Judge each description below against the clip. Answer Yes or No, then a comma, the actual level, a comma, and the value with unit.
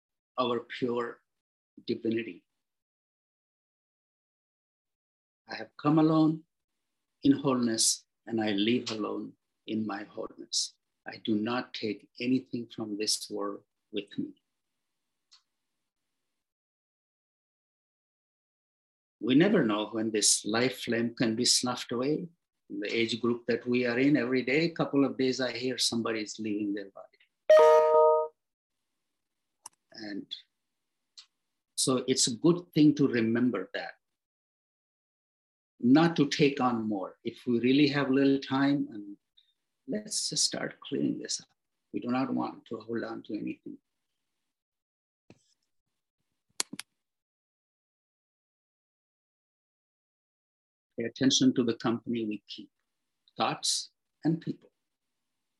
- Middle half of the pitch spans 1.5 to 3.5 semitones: No, average, 4.2 semitones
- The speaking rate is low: Yes, slow, 110 wpm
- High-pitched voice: No, low, 125 Hz